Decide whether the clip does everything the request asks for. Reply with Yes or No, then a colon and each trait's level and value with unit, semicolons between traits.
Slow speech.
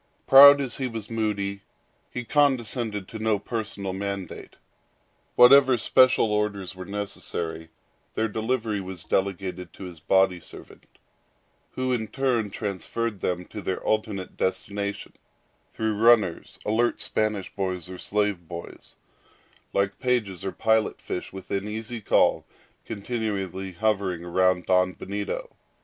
Yes: slow, 125 wpm